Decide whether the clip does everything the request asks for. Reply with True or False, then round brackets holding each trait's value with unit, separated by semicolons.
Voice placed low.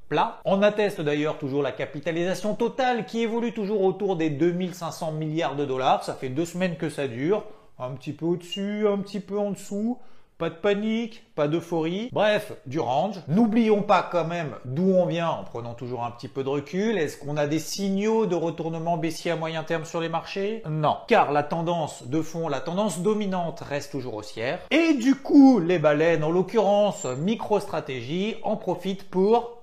False (175 Hz)